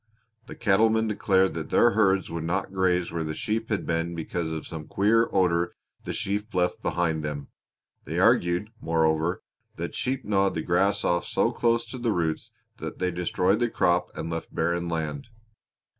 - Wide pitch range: No, average, 3.9 semitones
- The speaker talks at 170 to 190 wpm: Yes, average, 175 wpm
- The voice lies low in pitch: Yes, very low, 90 Hz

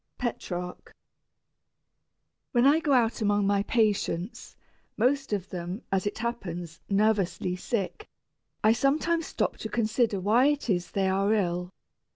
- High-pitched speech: Yes, high, 210 Hz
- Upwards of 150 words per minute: No, slow, 135 wpm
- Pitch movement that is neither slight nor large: Yes, average, 4.4 semitones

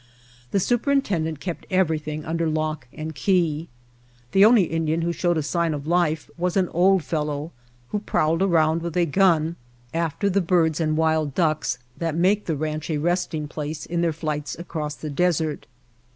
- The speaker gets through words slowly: No, average, 170 wpm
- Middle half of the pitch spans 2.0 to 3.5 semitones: Yes, narrow, 2.4 semitones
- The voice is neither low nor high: Yes, medium, 160 Hz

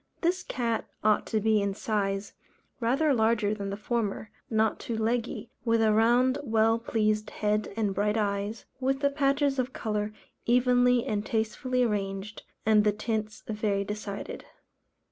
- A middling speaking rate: Yes, average, 150 wpm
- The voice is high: Yes, high, 220 Hz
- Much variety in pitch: No, narrow, 2.6 semitones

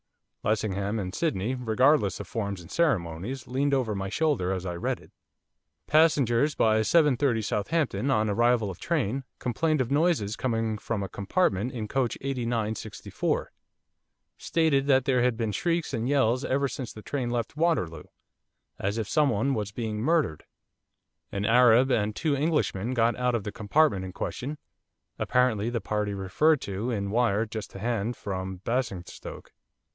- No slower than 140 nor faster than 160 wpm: Yes, average, 155 wpm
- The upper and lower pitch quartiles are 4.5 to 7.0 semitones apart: Yes, average, 4.8 semitones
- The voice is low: Yes, low, 115 Hz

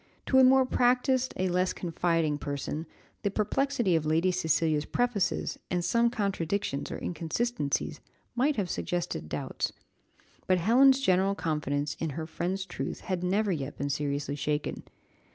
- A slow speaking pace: No, average, 145 wpm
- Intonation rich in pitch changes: Yes, wide, 6.4 semitones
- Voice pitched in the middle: Yes, medium, 180 Hz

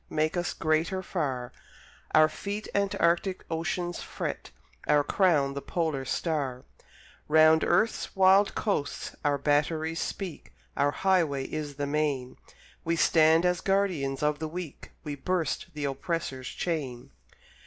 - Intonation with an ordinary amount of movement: Yes, average, 3.7 semitones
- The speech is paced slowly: Yes, slow, 130 wpm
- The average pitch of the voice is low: No, medium, 155 Hz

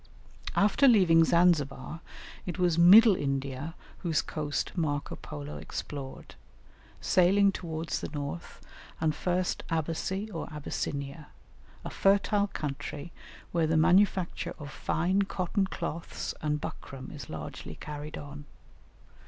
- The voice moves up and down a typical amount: Yes, average, 4.0 semitones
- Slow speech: Yes, slow, 115 wpm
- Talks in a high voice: No, medium, 165 Hz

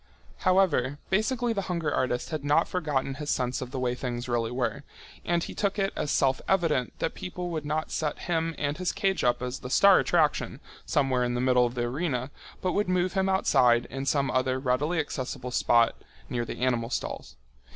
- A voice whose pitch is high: No, medium, 145 Hz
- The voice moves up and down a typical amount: No, wide, 5.8 semitones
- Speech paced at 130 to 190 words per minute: No, average, 200 wpm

